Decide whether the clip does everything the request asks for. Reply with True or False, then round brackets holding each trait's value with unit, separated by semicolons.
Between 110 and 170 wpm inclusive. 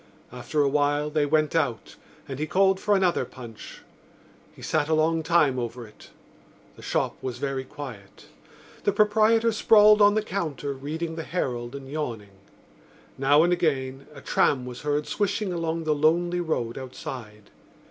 True (160 wpm)